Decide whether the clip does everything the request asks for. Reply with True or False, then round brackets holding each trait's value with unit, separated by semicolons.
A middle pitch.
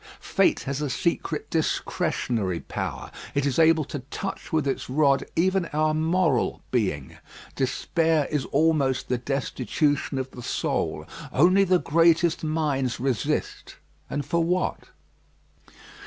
True (150 Hz)